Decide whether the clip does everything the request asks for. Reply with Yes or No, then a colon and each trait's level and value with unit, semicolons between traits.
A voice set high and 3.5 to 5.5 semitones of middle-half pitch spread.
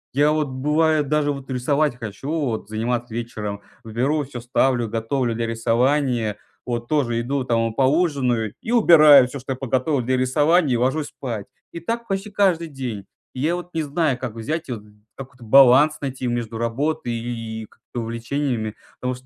No: low, 130 Hz; average, 4.2 semitones